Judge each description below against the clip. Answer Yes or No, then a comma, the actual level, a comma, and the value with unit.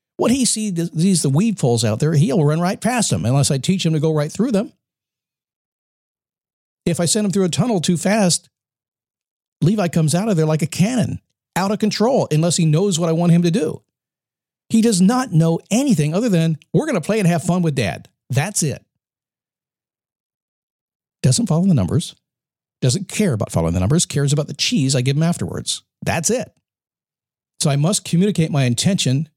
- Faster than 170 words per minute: Yes, average, 195 wpm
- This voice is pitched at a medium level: Yes, medium, 165 Hz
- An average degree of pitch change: Yes, average, 4.8 semitones